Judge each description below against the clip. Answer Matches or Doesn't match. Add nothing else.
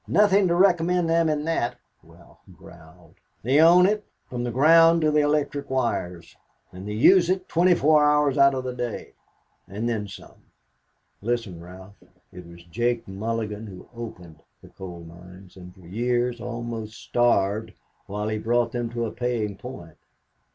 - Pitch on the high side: Doesn't match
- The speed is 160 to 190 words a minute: Matches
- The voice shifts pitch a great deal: Matches